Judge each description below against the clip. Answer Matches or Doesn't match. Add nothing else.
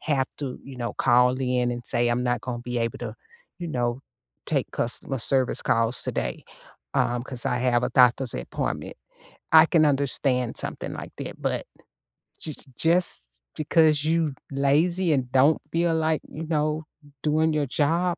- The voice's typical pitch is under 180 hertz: Matches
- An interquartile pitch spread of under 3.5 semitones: Doesn't match